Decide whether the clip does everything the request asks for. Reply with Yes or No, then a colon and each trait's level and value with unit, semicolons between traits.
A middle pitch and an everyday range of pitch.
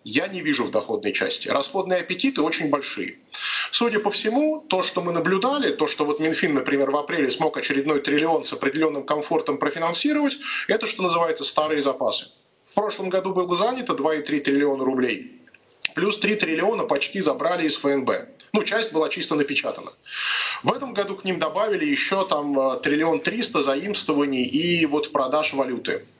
No: medium, 165 Hz; wide, 6.1 semitones